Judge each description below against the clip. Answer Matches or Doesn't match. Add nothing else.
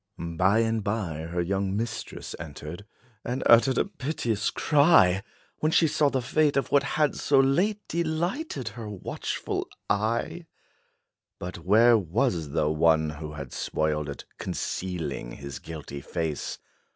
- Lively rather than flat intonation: Matches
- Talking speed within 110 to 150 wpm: Matches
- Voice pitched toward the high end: Doesn't match